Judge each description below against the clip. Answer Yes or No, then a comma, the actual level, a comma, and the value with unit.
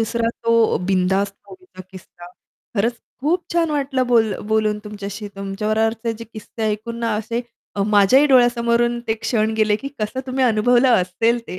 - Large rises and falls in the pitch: No, narrow, 2.6 semitones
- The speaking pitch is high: Yes, high, 225 Hz